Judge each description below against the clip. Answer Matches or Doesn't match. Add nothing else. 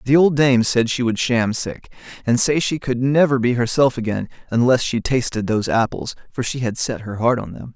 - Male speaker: Matches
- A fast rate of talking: Matches